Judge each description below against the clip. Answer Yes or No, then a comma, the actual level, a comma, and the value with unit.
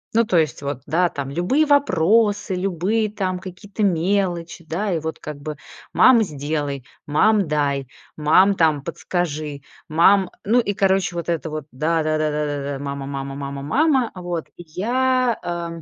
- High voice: No, medium, 170 Hz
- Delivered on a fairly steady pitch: No, average, 4.9 semitones